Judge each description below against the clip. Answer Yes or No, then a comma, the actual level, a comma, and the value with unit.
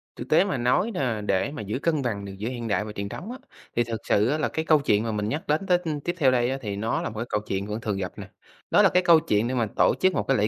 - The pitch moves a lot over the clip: Yes, wide, 6.6 semitones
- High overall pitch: No, low, 120 Hz